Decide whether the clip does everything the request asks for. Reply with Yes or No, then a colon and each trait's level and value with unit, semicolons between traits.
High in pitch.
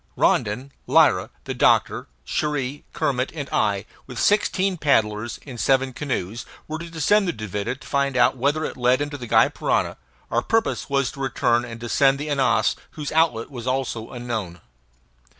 No: low, 130 Hz